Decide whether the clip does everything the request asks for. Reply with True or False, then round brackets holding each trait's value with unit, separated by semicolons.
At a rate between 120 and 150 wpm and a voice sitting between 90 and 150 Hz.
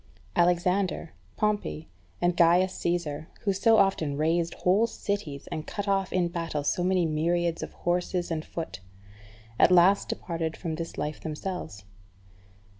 False (140 wpm; 175 Hz)